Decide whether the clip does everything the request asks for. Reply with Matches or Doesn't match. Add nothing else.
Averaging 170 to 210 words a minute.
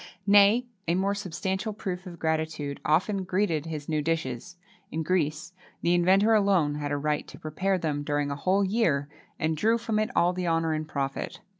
Matches